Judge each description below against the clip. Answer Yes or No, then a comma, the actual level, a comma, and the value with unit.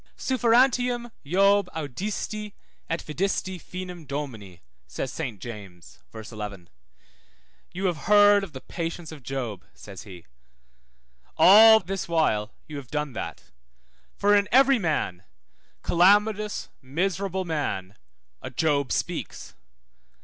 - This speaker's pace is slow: Yes, slow, 115 wpm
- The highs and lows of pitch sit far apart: Yes, wide, 8.0 semitones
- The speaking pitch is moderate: Yes, medium, 165 Hz